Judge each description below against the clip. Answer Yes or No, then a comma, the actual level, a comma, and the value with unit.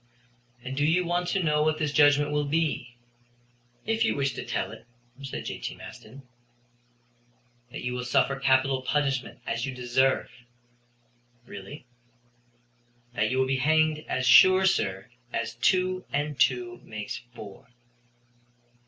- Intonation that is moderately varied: Yes, average, 3.7 semitones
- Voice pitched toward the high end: No, low, 135 Hz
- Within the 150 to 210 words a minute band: No, average, 140 wpm